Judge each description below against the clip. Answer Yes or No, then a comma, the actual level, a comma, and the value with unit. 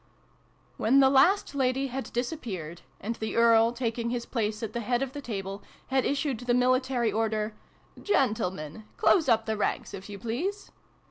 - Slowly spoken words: No, average, 180 wpm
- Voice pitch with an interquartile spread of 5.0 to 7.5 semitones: No, average, 3.4 semitones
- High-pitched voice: Yes, high, 235 Hz